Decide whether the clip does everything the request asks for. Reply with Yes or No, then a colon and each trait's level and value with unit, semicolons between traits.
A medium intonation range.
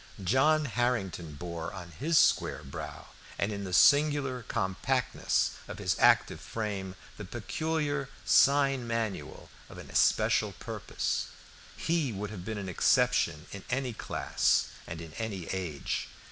No: wide, 6.6 semitones